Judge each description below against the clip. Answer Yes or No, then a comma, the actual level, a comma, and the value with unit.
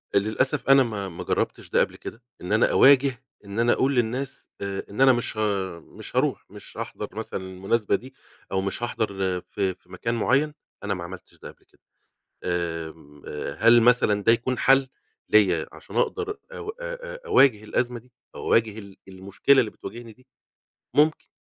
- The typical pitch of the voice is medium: No, low, 115 Hz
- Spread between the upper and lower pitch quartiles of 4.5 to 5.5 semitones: Yes, average, 5.0 semitones